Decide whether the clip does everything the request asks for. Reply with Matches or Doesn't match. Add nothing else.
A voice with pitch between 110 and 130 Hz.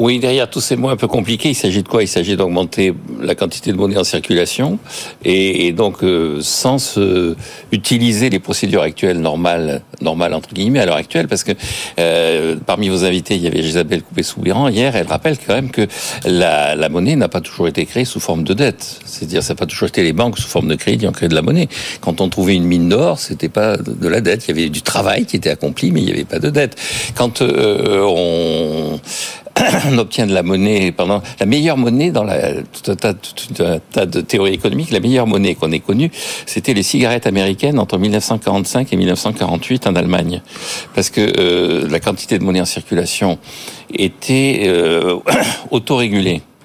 Doesn't match